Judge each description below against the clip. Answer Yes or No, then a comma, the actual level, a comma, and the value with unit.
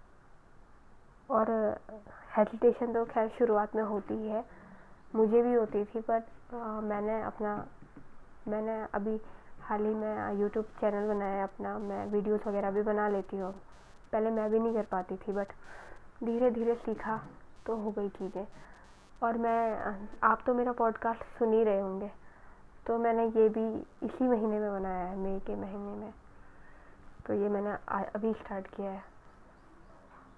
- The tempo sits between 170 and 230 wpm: No, average, 155 wpm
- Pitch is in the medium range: No, high, 215 Hz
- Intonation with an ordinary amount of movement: No, narrow, 1.8 semitones